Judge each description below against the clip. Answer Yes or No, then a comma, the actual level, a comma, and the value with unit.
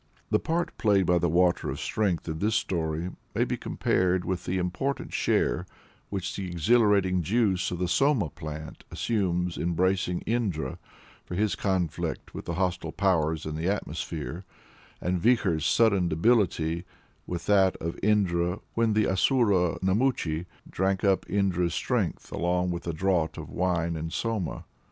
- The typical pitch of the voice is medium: No, very low, 90 Hz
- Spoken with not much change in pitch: No, average, 3.0 semitones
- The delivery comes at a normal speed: Yes, average, 155 wpm